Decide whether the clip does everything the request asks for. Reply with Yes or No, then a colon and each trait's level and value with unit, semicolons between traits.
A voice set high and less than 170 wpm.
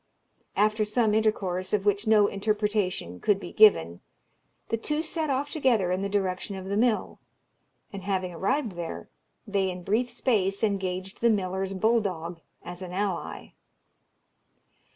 Yes: high, 200 Hz; average, 150 wpm